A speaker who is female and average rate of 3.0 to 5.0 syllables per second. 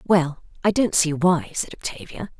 Yes: female; 4.5 syllables/s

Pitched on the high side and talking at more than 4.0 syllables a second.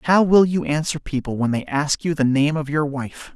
No: medium, 150 Hz; 5.0 syllables/s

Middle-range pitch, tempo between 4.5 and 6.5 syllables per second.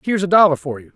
No: medium, 165 Hz; 8.2 syllables/s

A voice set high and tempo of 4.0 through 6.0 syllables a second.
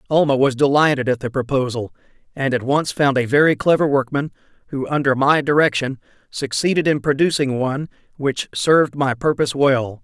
No: low, 135 Hz; 5.5 syllables/s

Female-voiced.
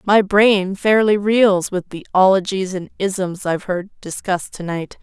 Yes: female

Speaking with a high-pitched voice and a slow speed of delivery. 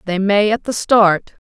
No: high, 205 Hz; fast, 205 wpm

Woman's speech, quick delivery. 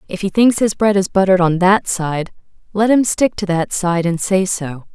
Yes: female; fast, 230 wpm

